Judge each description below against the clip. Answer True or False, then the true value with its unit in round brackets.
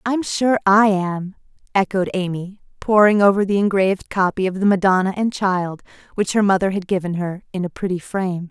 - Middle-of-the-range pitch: False (195 Hz)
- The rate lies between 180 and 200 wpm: True (185 wpm)